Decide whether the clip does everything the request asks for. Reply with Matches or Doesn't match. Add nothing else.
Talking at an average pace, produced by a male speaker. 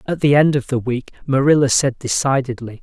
Matches